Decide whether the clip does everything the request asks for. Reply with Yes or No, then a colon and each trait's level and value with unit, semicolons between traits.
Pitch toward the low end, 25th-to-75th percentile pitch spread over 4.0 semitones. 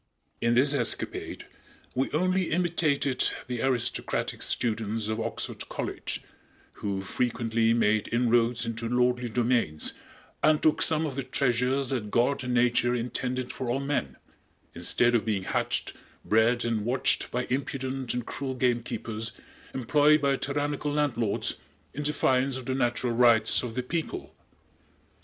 No: low, 125 Hz; average, 2.8 semitones